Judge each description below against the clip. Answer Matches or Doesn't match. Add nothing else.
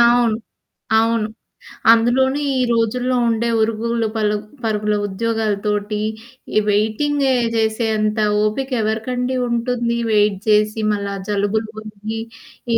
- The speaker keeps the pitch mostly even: Matches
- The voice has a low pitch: Doesn't match